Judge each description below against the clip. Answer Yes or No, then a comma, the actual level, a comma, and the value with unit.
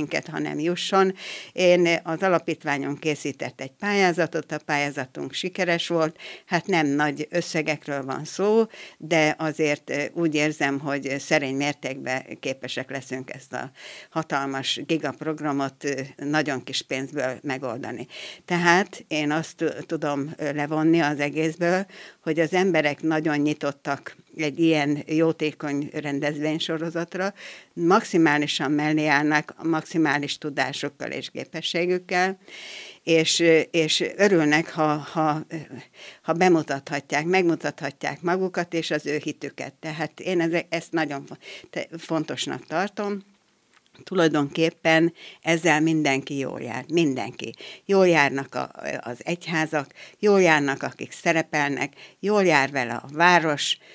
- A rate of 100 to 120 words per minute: Yes, average, 110 wpm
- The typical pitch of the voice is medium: Yes, medium, 155 Hz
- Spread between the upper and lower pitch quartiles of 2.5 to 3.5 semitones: Yes, average, 2.8 semitones